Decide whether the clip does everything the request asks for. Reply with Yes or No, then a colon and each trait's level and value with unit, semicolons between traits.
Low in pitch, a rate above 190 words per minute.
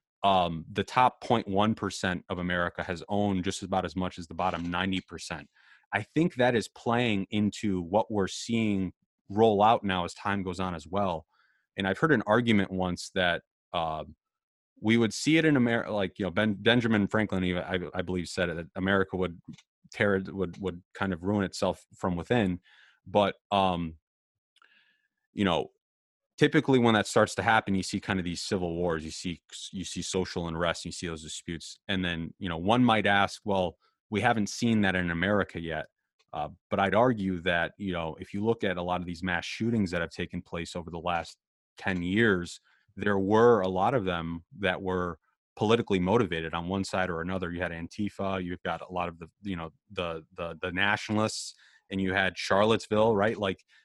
Yes: very low, 95 Hz; average, 200 wpm